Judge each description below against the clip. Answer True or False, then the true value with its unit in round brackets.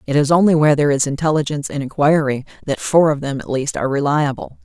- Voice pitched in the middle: True (145 Hz)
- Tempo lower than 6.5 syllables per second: False (6.8 syllables/s)